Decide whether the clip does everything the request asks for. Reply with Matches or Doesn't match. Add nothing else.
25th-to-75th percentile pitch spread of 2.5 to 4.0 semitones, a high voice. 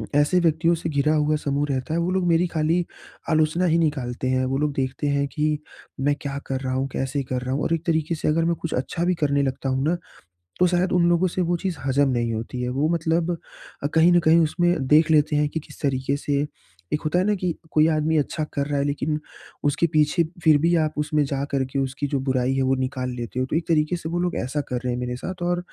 Doesn't match